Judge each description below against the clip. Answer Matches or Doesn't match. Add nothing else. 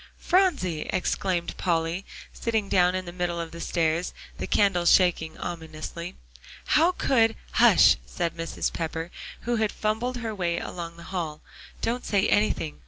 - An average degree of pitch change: Matches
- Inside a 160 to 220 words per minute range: Doesn't match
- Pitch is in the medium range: Matches